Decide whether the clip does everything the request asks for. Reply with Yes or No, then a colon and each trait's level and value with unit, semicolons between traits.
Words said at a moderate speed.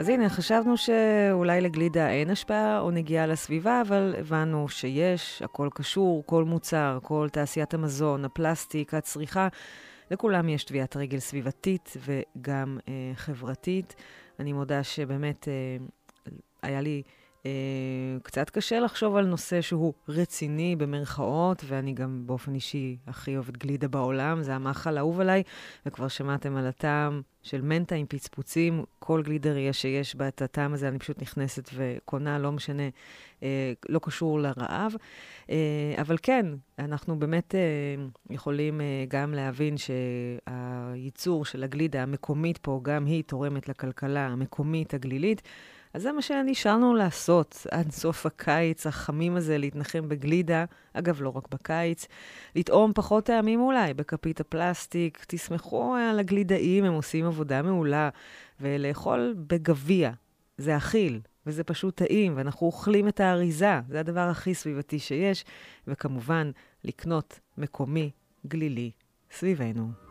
Yes: average, 125 wpm